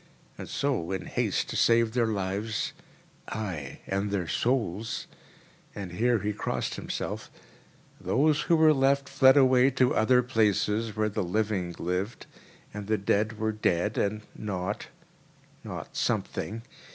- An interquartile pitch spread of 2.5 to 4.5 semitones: Yes, average, 3.9 semitones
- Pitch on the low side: Yes, low, 110 Hz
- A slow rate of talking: Yes, slow, 130 wpm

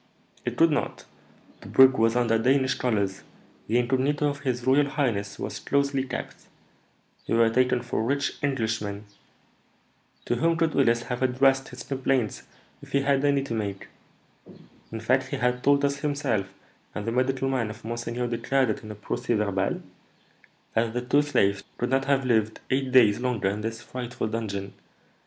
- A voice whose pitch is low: Yes, low, 125 Hz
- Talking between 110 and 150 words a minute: No, average, 170 wpm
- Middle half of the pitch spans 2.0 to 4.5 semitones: Yes, average, 3.3 semitones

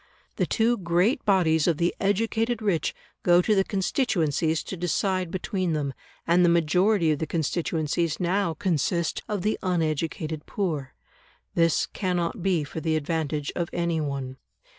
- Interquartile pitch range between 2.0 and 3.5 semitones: Yes, average, 3.2 semitones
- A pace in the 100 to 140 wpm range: No, average, 150 wpm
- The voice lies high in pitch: No, medium, 170 Hz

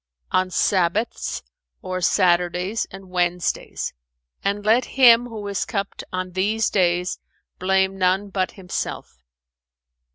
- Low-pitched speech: No, high, 190 Hz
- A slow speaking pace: Yes, slow, 110 wpm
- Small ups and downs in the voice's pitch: Yes, narrow, 2.2 semitones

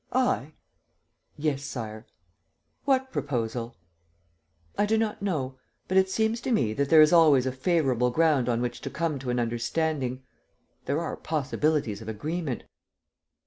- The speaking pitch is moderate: Yes, medium, 145 Hz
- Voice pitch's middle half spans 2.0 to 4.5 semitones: No, average, 5.3 semitones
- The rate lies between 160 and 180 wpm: No, average, 145 wpm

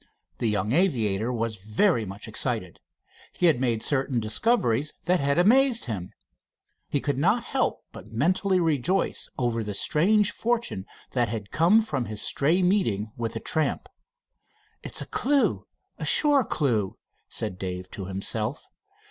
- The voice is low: Yes, low, 130 Hz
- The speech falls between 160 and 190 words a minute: No, average, 150 wpm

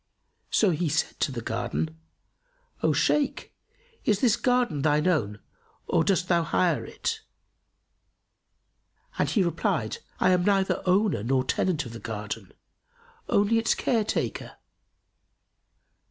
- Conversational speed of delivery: No, slow, 125 wpm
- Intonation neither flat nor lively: No, wide, 7.4 semitones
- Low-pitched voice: No, medium, 175 Hz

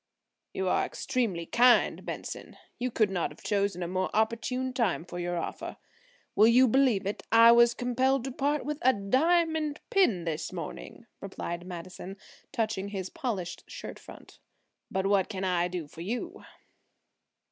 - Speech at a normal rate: Yes, average, 155 wpm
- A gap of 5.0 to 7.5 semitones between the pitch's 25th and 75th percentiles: Yes, wide, 5.6 semitones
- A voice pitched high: Yes, high, 215 Hz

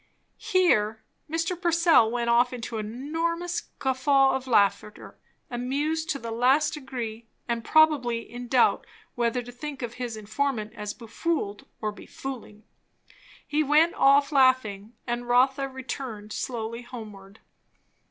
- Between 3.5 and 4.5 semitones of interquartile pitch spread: Yes, average, 3.8 semitones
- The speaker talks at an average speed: No, slow, 130 wpm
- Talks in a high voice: Yes, high, 245 Hz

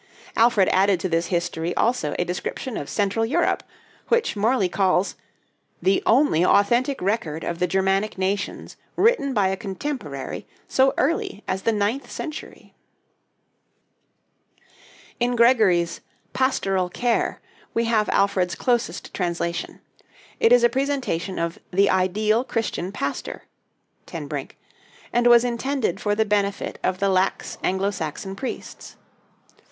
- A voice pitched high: Yes, high, 200 Hz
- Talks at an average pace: No, slow, 130 wpm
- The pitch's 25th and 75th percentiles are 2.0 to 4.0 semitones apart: No, average, 4.5 semitones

